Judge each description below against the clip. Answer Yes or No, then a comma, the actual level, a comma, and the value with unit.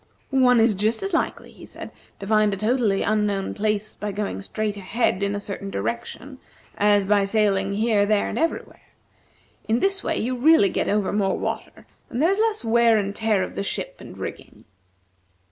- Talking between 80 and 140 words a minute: No, average, 190 wpm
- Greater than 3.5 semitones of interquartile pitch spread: No, average, 2.9 semitones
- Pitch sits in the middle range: No, high, 210 Hz